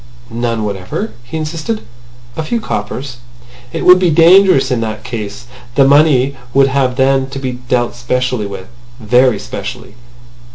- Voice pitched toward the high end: No, low, 125 Hz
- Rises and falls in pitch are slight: No, average, 3.5 semitones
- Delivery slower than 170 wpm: Yes, average, 150 wpm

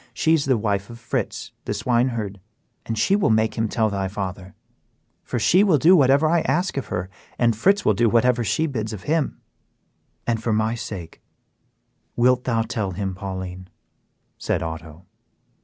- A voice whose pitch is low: Yes, low, 115 Hz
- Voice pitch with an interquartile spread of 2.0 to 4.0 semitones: No, average, 4.8 semitones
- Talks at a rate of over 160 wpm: Yes, average, 175 wpm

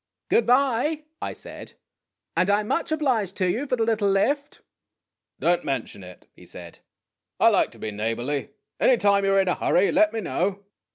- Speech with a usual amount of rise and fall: No, wide, 6.2 semitones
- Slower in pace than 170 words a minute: No, fast, 205 wpm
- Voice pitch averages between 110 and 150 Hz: No, high, 200 Hz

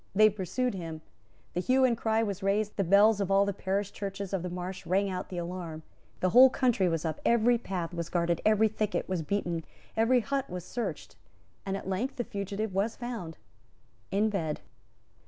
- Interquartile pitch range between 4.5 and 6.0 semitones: No, average, 3.4 semitones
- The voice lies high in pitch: Yes, high, 195 Hz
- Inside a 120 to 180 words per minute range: No, average, 190 wpm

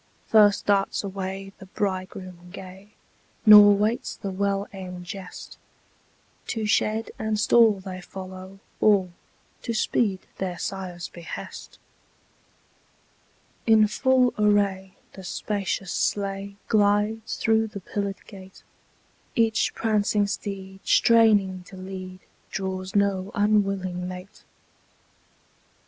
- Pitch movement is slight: Yes, narrow, 2.0 semitones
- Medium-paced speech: No, slow, 105 wpm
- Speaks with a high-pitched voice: Yes, high, 195 Hz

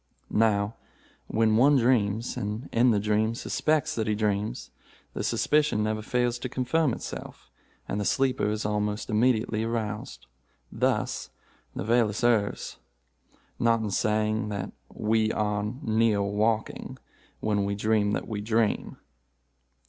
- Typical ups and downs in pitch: No, narrow, 1.9 semitones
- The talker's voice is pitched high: No, low, 110 Hz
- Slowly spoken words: Yes, slow, 130 wpm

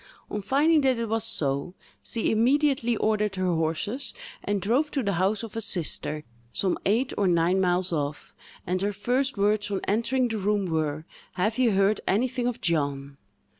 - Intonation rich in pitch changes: No, average, 4.7 semitones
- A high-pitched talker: Yes, high, 205 Hz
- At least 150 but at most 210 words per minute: Yes, average, 175 wpm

